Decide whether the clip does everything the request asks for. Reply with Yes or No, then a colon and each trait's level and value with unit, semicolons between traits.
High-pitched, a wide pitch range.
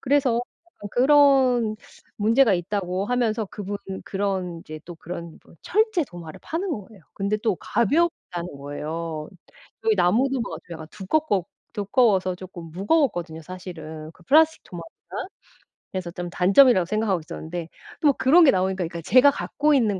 Yes: high, 195 Hz; wide, 6.4 semitones